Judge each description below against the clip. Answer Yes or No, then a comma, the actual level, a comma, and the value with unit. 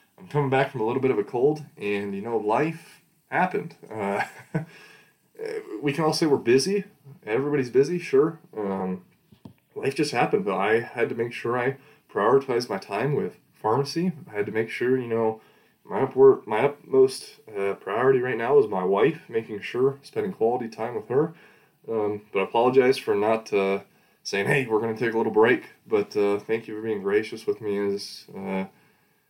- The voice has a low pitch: No, medium, 145 Hz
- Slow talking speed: No, average, 190 wpm